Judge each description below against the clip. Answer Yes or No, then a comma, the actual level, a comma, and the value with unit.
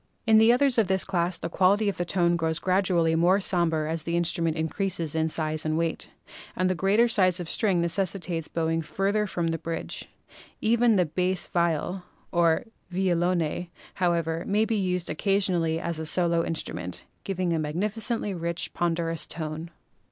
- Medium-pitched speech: Yes, medium, 175 Hz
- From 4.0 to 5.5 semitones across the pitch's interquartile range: No, average, 2.8 semitones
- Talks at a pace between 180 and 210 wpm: No, average, 165 wpm